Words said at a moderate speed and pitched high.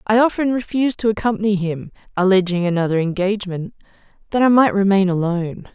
Yes: average, 145 wpm; high, 200 Hz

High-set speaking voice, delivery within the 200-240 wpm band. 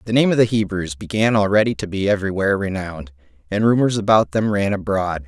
No: low, 100 Hz; fast, 205 wpm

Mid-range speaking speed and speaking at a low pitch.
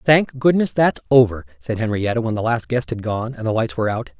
No: fast, 245 wpm; low, 115 Hz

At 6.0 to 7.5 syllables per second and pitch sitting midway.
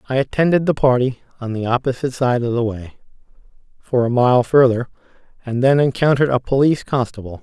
No: 6.1 syllables/s; low, 125 Hz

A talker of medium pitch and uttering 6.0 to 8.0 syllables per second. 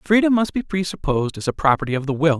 Yes: medium, 165 Hz; 6.8 syllables/s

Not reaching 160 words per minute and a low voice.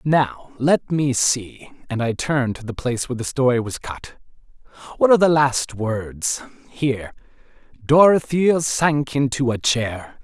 Yes: average, 150 wpm; low, 130 Hz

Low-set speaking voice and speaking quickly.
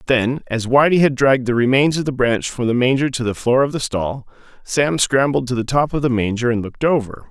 Yes: low, 130 Hz; fast, 245 wpm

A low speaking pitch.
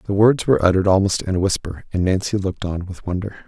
Yes: very low, 95 Hz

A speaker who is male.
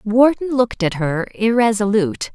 No: female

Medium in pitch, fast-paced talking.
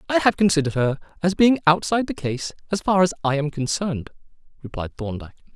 No: medium, 165 Hz; average, 185 wpm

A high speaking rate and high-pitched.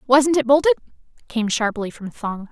No: average, 165 wpm; high, 245 Hz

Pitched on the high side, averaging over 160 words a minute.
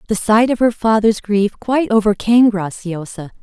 No: high, 215 Hz; average, 155 wpm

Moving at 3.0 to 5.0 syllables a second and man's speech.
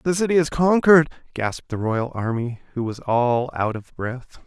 Yes: 4.8 syllables/s; male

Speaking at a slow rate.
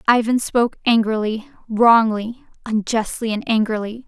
Yes: slow, 105 wpm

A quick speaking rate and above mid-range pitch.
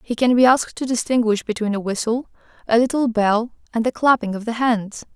Yes: fast, 210 wpm; high, 230 Hz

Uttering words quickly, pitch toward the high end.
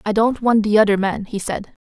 Yes: fast, 255 wpm; high, 210 Hz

